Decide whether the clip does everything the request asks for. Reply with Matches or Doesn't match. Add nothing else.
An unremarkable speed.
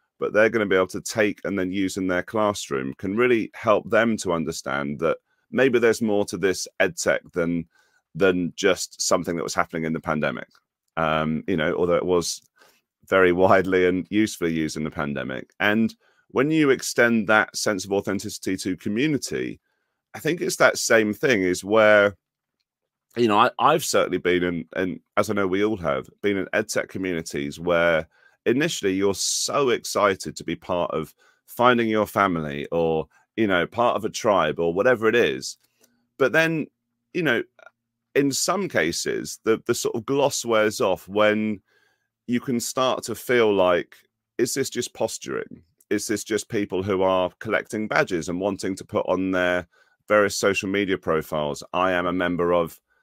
Matches